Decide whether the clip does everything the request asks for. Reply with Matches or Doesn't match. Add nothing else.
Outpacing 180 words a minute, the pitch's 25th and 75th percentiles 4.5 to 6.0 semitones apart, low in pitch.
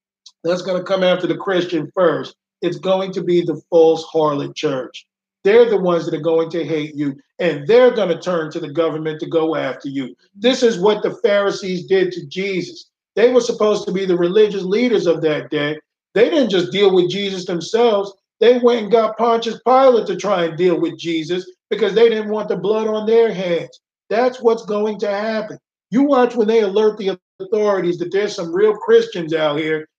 Doesn't match